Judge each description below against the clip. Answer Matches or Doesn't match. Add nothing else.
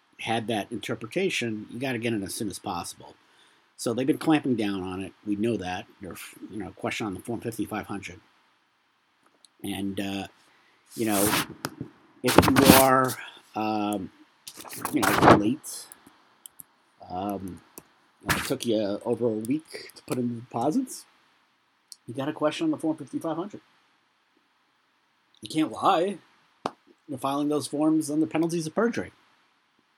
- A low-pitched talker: Matches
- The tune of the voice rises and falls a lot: Matches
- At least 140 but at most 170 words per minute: Matches